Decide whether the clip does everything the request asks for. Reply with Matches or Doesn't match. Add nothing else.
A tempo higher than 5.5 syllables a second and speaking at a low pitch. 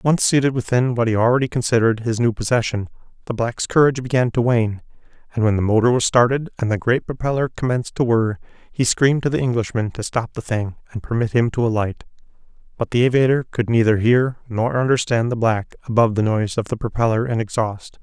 Matches